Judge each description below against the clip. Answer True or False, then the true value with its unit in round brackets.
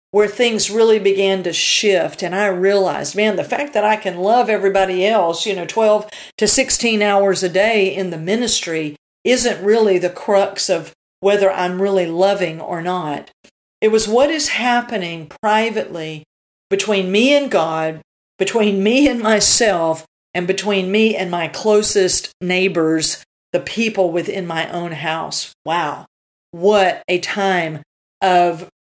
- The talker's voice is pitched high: True (195 Hz)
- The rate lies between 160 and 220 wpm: False (150 wpm)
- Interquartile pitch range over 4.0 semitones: False (3.3 semitones)